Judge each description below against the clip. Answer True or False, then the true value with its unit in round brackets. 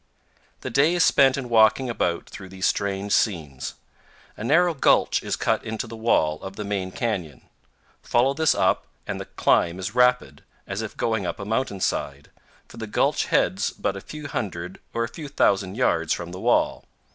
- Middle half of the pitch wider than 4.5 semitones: True (5.0 semitones)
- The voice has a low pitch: True (105 Hz)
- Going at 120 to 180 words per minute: False (190 wpm)